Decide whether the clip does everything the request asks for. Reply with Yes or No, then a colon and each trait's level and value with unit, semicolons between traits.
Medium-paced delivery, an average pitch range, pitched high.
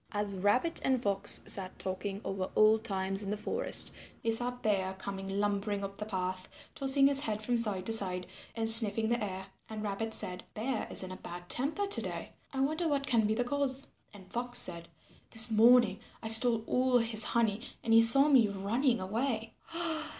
Yes: average, 195 wpm; average, 3.7 semitones; high, 220 Hz